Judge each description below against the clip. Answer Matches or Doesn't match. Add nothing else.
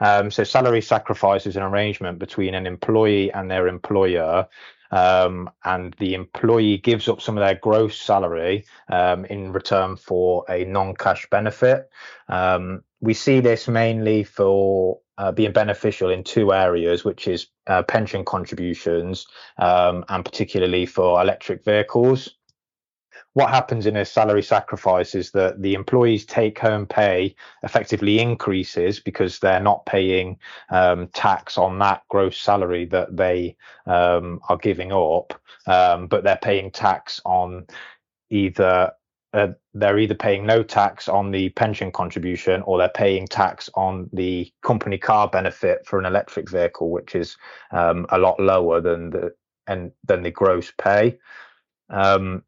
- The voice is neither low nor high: Doesn't match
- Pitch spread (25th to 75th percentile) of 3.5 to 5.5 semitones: Doesn't match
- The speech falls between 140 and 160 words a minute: Matches